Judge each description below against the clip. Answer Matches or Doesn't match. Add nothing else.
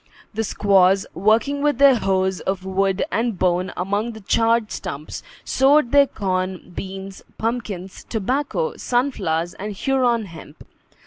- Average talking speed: Doesn't match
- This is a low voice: Doesn't match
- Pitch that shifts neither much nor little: Matches